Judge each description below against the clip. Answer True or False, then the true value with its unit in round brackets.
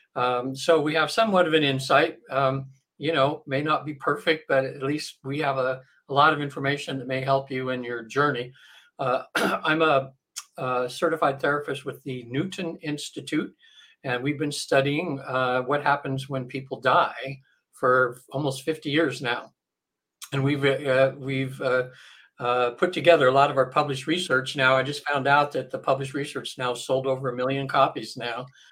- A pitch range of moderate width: False (2.0 semitones)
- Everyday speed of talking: True (180 wpm)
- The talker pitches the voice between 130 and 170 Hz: True (135 Hz)